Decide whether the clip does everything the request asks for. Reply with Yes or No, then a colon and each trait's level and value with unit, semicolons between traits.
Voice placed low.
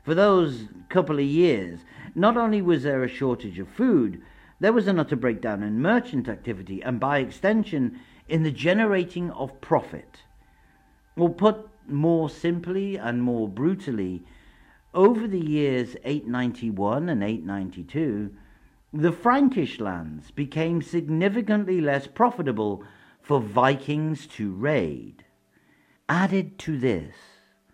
No: medium, 145 Hz